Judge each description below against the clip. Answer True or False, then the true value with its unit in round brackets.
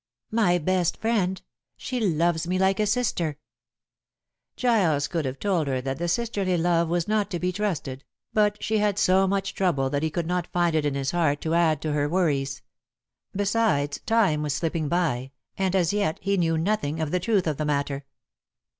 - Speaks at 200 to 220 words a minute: False (190 wpm)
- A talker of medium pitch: True (175 Hz)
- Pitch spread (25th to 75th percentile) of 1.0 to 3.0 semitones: False (4.6 semitones)